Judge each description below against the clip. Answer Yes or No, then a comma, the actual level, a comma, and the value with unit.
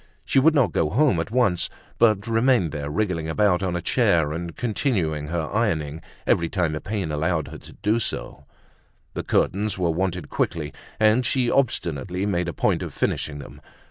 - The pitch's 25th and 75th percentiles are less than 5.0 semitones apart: No, average, 5.3 semitones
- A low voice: Yes, very low, 90 Hz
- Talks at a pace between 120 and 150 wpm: No, average, 180 wpm